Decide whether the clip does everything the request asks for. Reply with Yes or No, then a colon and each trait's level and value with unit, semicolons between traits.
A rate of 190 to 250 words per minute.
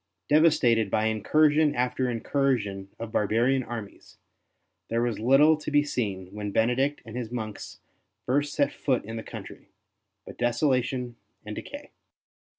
No: average, 140 wpm